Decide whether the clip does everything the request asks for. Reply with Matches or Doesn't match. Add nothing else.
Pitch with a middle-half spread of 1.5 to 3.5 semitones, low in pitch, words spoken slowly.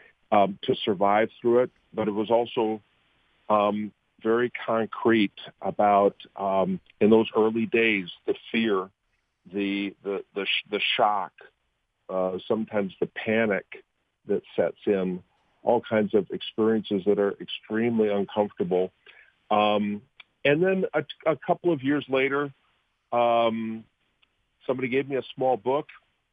Matches